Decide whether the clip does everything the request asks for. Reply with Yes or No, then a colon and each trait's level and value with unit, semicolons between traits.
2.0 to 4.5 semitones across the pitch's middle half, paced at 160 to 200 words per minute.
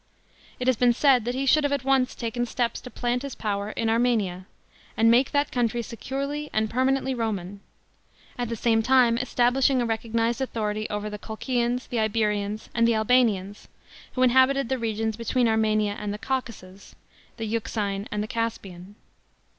Yes: average, 2.9 semitones; average, 170 wpm